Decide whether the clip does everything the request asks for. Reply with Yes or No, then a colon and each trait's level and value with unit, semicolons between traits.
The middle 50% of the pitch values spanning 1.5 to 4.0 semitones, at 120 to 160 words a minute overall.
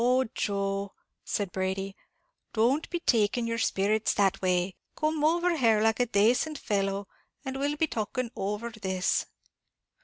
No: average, 4.7 semitones; average, 145 wpm